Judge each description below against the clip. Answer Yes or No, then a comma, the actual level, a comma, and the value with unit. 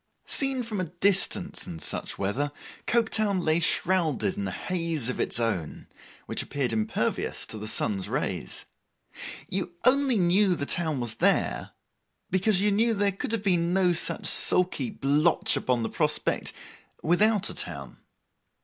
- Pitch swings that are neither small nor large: No, wide, 6.1 semitones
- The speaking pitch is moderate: Yes, medium, 180 Hz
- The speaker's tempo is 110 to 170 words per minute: Yes, average, 150 wpm